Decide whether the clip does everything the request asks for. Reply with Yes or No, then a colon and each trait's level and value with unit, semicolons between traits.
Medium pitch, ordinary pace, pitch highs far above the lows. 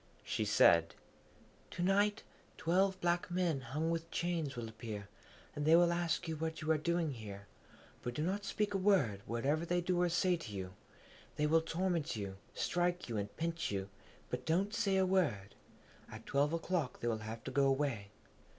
Yes: medium, 160 Hz; average, 180 wpm; wide, 6.9 semitones